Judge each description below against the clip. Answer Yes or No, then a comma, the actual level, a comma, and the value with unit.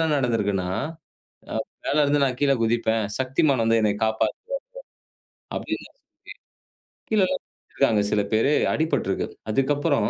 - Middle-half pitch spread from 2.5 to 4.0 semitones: No, average, 4.6 semitones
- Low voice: Yes, low, 130 Hz